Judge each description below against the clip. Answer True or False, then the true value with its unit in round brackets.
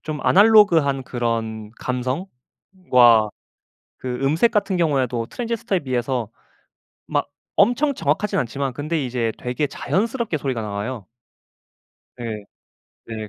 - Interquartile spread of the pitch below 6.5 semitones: False (7.3 semitones)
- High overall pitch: False (135 Hz)